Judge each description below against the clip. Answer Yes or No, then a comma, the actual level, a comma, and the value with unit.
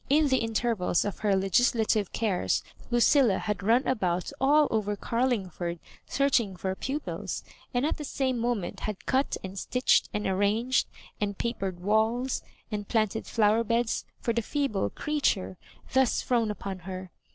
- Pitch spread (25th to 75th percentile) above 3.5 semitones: Yes, average, 4.3 semitones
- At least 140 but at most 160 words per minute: Yes, average, 150 wpm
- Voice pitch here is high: Yes, high, 220 Hz